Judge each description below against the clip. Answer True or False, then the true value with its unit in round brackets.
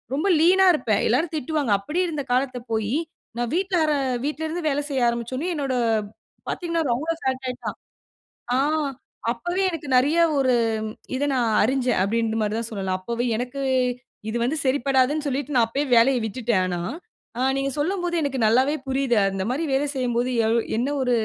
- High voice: True (260 Hz)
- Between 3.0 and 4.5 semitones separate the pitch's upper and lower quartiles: True (4.1 semitones)